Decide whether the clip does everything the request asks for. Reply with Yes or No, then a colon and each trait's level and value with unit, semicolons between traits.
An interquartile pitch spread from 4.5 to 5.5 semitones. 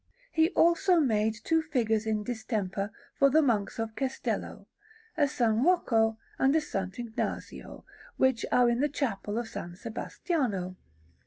Yes: average, 5.0 semitones